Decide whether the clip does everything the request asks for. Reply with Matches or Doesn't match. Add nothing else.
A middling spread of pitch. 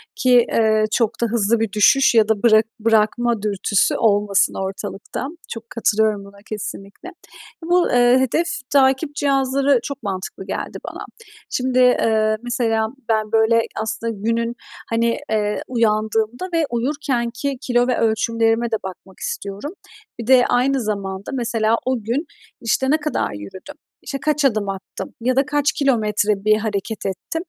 Matches